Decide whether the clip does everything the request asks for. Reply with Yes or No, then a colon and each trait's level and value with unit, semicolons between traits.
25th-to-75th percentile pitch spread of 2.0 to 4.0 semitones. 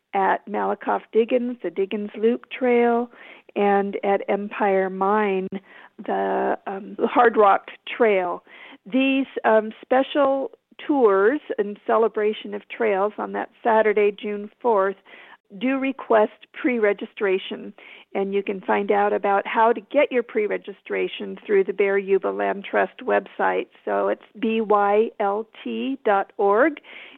Yes: average, 3.0 semitones